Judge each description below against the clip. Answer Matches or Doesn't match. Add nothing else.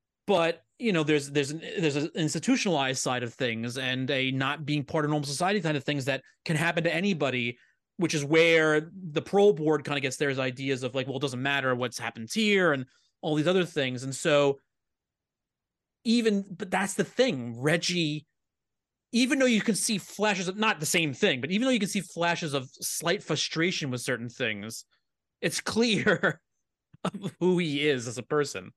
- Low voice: Doesn't match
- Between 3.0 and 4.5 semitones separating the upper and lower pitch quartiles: Doesn't match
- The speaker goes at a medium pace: Matches